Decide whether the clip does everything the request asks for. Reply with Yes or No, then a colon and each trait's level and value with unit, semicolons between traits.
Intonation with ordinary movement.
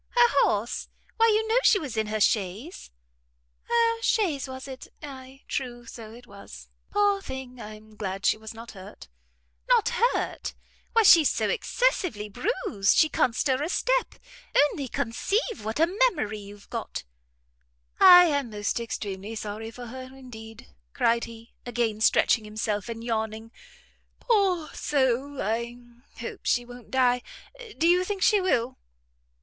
No: wide, 7.3 semitones